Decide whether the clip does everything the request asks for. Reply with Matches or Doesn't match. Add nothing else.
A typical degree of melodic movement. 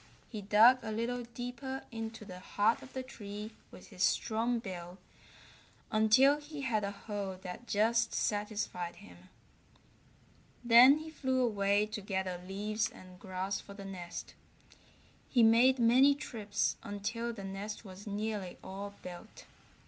Matches